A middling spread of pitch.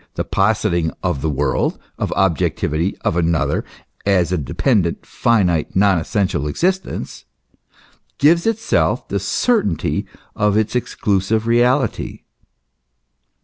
No: wide, 5.8 semitones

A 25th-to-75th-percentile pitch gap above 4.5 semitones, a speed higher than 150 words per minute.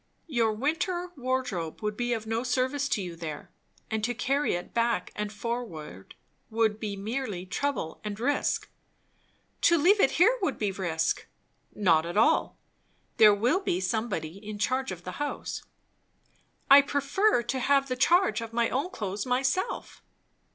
Yes: wide, 5.4 semitones; average, 160 wpm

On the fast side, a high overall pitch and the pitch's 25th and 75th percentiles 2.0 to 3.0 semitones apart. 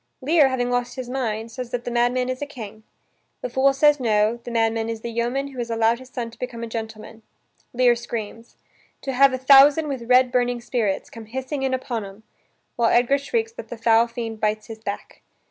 Yes: fast, 215 wpm; high, 240 Hz; narrow, 2.4 semitones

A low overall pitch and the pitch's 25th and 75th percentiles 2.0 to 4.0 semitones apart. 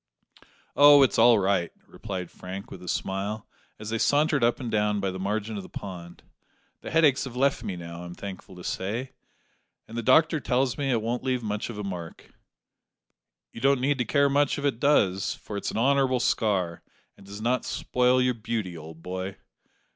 No: low, 110 Hz; average, 5.2 semitones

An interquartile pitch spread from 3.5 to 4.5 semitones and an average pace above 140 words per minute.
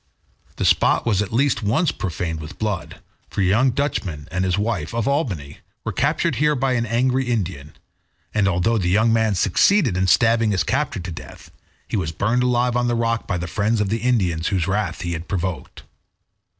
No: average, 5.0 semitones; average, 200 wpm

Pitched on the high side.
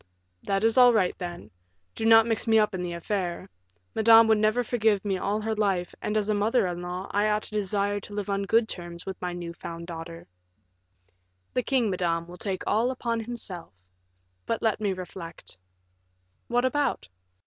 Yes: high, 205 Hz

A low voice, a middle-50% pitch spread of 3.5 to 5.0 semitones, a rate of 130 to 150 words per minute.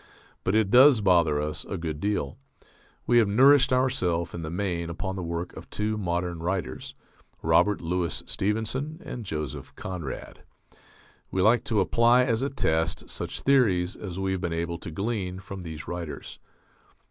No: very low, 95 Hz; average, 4.7 semitones; average, 165 wpm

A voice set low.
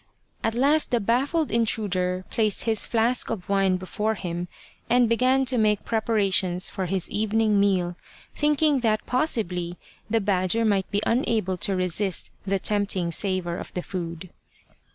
No: high, 205 Hz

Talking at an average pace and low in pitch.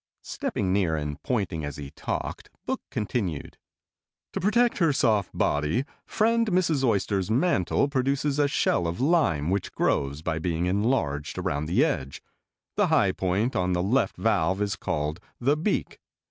Yes: average, 155 wpm; low, 100 Hz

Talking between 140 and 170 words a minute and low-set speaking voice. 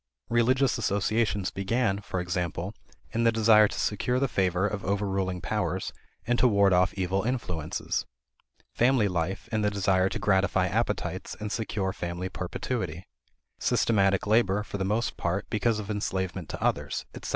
Yes: average, 155 wpm; low, 100 Hz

